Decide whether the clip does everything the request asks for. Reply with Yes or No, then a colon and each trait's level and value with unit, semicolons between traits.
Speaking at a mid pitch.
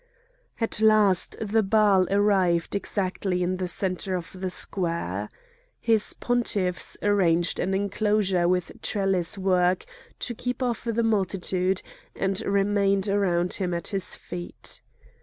No: high, 195 Hz